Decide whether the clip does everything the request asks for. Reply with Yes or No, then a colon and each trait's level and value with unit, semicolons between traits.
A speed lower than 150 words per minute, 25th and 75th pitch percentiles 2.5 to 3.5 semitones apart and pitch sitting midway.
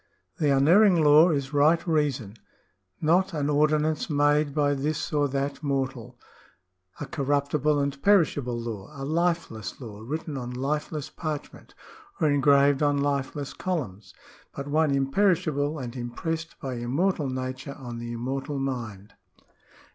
Yes: average, 140 wpm; average, 2.8 semitones; medium, 145 Hz